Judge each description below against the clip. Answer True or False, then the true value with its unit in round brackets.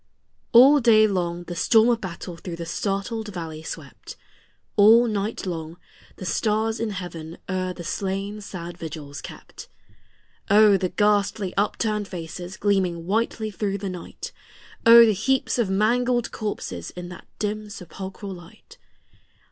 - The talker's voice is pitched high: True (195 Hz)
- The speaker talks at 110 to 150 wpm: True (140 wpm)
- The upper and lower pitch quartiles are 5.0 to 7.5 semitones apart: False (3.6 semitones)